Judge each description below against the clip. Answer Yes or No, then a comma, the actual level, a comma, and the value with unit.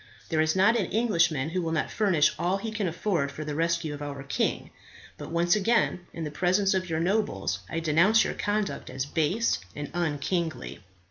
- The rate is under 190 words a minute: No, average, 195 wpm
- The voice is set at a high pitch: No, medium, 170 Hz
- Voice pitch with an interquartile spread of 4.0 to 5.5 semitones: Yes, average, 4.4 semitones